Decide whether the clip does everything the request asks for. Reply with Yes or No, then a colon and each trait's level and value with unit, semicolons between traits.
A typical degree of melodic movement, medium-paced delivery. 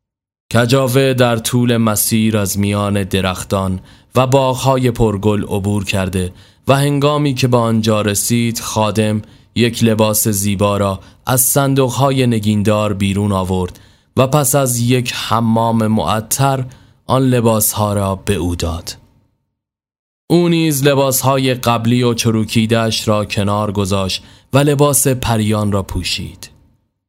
Yes: average, 3.8 semitones; average, 120 wpm